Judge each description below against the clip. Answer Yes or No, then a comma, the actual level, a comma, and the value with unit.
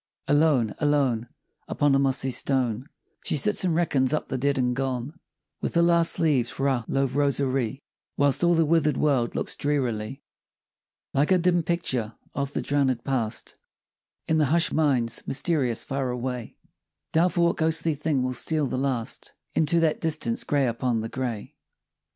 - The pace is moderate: Yes, average, 160 wpm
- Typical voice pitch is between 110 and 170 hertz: Yes, medium, 140 Hz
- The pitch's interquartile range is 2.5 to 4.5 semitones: Yes, average, 3.8 semitones